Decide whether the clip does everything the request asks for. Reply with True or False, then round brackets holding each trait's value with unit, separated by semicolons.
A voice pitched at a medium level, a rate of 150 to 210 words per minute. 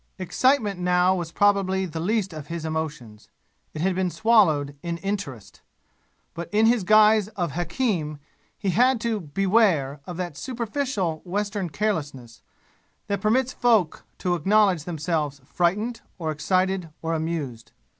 False (180 Hz; 135 wpm)